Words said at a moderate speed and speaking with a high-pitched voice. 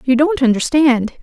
Yes: average, 145 wpm; very high, 270 Hz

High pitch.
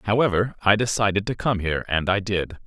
No: low, 100 Hz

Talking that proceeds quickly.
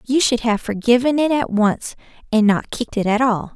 Yes: fast, 220 wpm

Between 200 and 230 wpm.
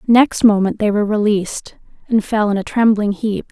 No: average, 190 wpm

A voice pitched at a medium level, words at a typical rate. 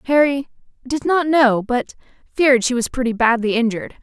No: very high, 255 Hz; average, 165 wpm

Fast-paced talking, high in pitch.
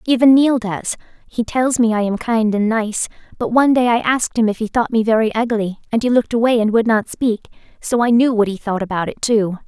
Yes: fast, 250 wpm; high, 225 Hz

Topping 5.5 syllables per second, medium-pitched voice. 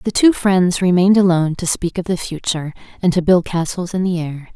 Yes: 5.7 syllables/s; medium, 180 Hz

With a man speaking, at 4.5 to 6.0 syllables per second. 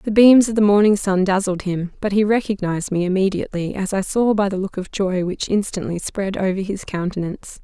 No: female; 5.7 syllables/s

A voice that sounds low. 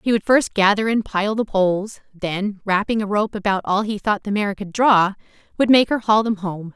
No: high, 205 Hz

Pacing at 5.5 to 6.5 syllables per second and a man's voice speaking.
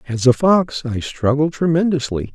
No: 4.7 syllables/s; male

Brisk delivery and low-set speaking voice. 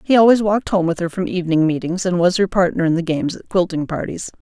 No: fast, 255 wpm; medium, 180 Hz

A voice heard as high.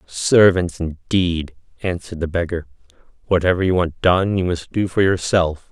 No: very low, 90 Hz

